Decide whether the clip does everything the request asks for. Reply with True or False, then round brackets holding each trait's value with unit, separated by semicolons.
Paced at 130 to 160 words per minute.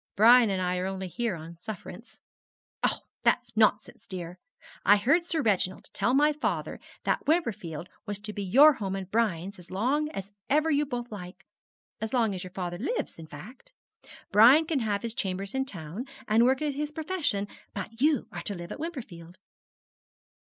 False (180 wpm)